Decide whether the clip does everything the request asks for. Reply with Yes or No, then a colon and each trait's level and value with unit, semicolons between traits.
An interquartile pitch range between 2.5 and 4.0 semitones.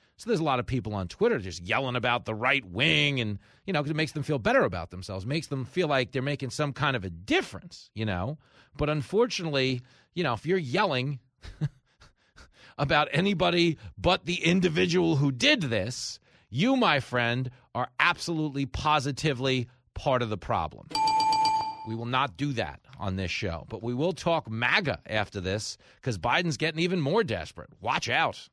No: wide, 5.5 semitones